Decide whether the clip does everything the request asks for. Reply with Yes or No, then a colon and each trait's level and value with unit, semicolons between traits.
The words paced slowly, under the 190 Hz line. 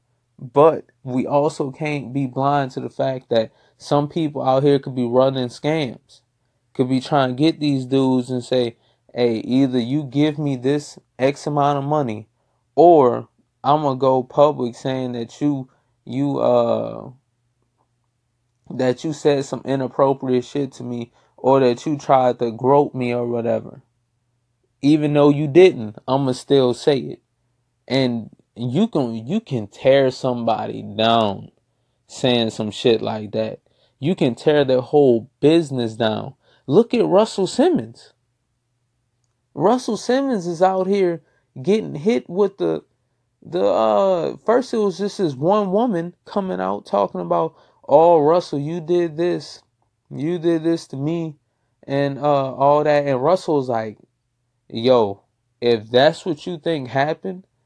No: average, 150 wpm; low, 135 Hz